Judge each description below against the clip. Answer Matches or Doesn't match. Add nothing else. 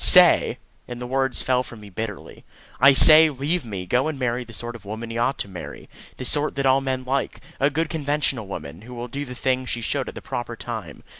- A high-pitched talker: Doesn't match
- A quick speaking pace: Matches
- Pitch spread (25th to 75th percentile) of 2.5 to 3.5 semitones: Matches